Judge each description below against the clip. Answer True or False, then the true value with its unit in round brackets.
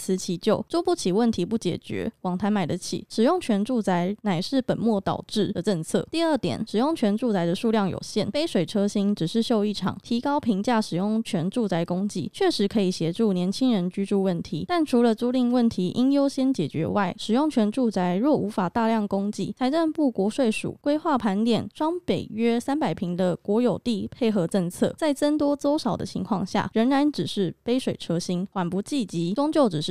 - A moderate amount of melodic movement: True (4.8 semitones)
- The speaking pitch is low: False (215 Hz)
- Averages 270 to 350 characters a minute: True (300 characters per minute)